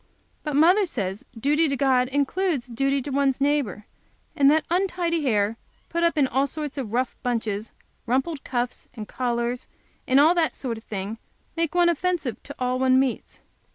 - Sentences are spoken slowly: No, average, 175 wpm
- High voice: Yes, very high, 270 Hz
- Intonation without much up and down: No, average, 4.4 semitones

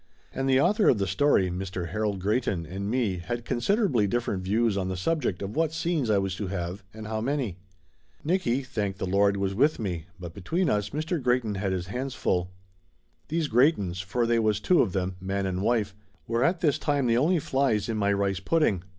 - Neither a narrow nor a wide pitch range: No, wide, 5.7 semitones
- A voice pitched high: No, low, 105 Hz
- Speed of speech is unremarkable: No, fast, 210 wpm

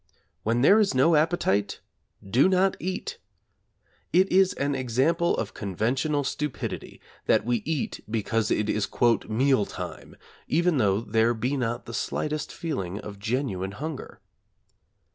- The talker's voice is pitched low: Yes, low, 130 Hz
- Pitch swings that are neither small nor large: No, wide, 6.3 semitones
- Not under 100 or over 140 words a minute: Yes, slow, 135 wpm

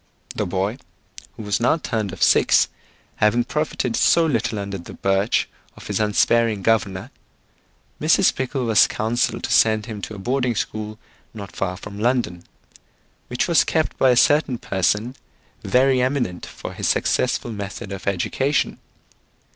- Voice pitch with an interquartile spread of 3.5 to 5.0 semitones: Yes, average, 3.9 semitones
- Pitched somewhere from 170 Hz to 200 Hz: No, low, 110 Hz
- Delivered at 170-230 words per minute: No, average, 150 wpm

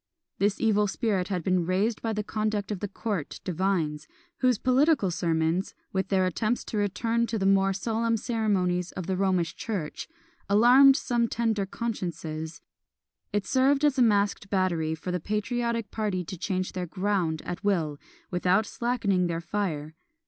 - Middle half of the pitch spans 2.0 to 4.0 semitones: Yes, average, 3.7 semitones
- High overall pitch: Yes, high, 195 Hz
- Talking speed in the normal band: Yes, average, 160 wpm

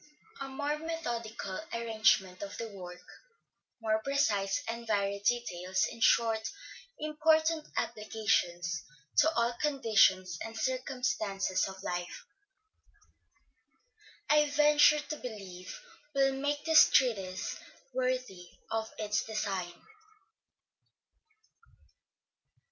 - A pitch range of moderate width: No, wide, 6.0 semitones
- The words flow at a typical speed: No, slow, 90 wpm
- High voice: Yes, high, 225 Hz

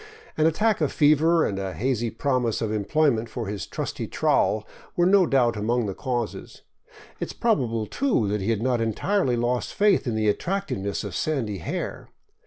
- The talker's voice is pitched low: Yes, low, 120 Hz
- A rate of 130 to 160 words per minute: No, average, 185 wpm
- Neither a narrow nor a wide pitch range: No, wide, 6.5 semitones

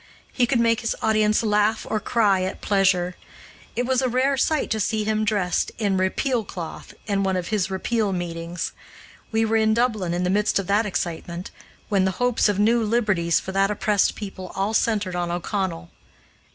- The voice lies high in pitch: Yes, high, 205 Hz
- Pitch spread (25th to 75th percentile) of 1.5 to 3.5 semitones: Yes, average, 3.0 semitones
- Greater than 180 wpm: Yes, average, 190 wpm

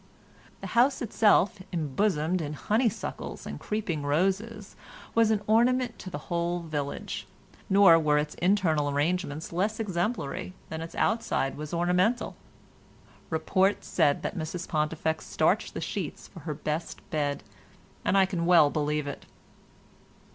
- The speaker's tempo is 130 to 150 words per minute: Yes, slow, 135 wpm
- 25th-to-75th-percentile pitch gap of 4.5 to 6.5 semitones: Yes, average, 5.1 semitones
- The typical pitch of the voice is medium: Yes, medium, 175 Hz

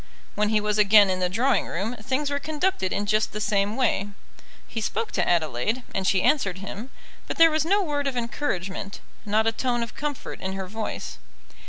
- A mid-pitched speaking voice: No, high, 215 Hz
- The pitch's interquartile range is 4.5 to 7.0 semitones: Yes, average, 5.2 semitones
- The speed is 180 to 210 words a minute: Yes, average, 200 wpm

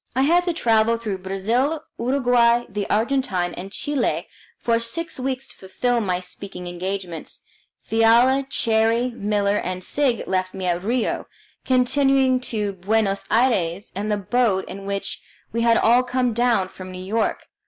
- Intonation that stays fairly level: No, average, 4.4 semitones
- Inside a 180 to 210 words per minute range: No, average, 155 wpm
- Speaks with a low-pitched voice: No, high, 225 Hz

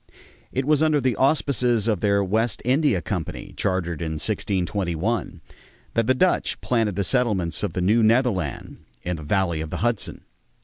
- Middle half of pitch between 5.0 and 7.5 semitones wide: Yes, wide, 5.5 semitones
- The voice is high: No, low, 105 Hz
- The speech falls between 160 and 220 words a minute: Yes, average, 165 wpm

